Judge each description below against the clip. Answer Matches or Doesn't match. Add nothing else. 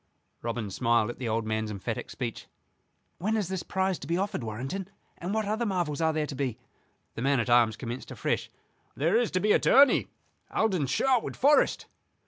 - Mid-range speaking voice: Matches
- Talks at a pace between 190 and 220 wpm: Matches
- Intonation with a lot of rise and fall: Matches